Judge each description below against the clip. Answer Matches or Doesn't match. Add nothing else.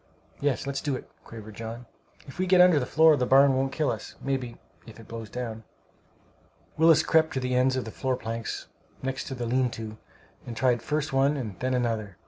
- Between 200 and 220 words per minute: Matches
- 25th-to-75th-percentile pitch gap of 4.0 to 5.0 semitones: Doesn't match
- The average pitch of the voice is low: Matches